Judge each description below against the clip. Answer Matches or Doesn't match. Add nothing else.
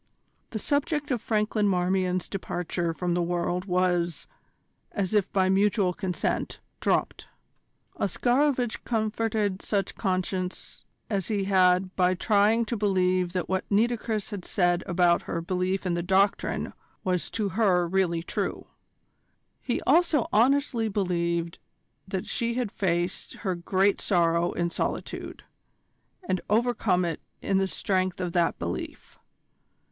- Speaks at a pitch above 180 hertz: Matches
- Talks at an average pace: Doesn't match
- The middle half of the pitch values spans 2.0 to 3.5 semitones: Matches